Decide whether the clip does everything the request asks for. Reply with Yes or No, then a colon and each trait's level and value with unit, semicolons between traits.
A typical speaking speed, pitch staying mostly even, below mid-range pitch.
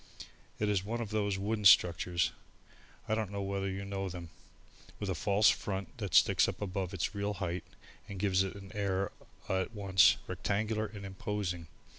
Yes: average, 175 wpm; narrow, 1.6 semitones; low, 100 Hz